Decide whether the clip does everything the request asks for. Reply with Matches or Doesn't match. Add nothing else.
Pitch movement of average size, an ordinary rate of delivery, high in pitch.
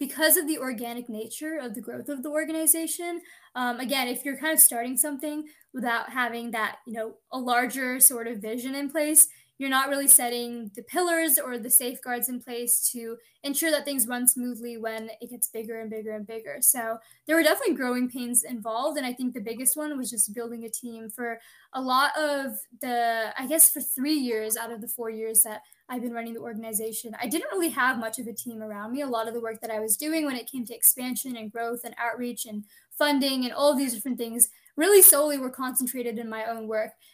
Doesn't match